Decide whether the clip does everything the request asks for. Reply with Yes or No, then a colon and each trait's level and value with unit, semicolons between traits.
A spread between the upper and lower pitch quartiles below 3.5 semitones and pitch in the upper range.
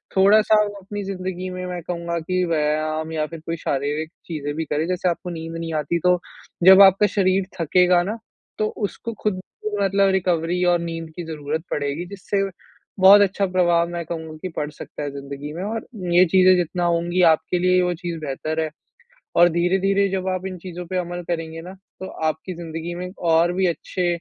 No: narrow, 2.5 semitones; medium, 175 Hz